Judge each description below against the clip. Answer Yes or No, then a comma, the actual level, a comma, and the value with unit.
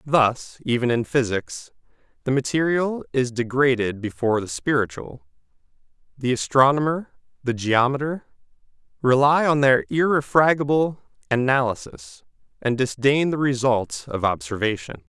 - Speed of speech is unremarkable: No, slow, 105 wpm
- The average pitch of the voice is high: No, low, 130 Hz